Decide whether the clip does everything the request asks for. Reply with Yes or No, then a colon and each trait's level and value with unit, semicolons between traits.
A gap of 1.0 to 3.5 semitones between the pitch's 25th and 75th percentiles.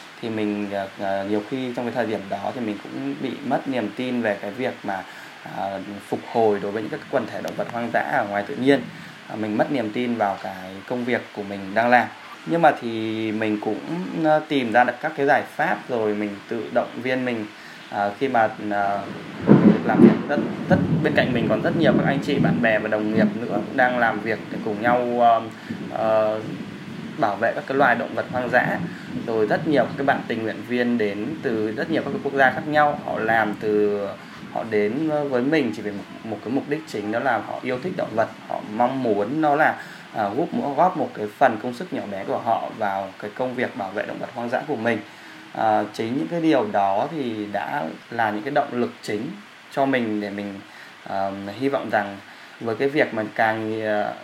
Yes: average, 3.1 semitones